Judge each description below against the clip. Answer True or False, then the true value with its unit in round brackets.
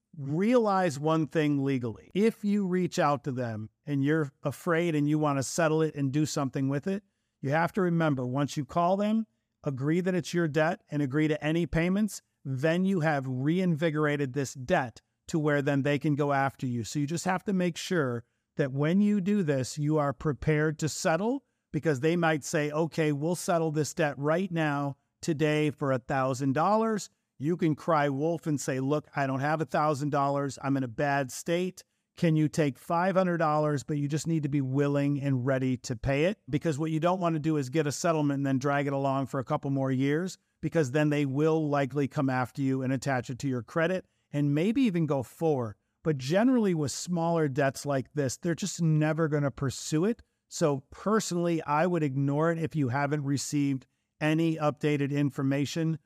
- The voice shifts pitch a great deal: False (3.0 semitones)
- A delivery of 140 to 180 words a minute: False (200 wpm)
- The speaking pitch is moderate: True (150 Hz)